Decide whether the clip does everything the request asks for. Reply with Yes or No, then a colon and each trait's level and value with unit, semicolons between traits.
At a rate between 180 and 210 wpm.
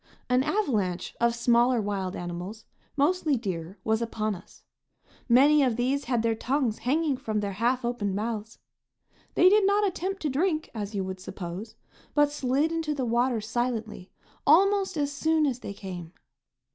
No: average, 160 wpm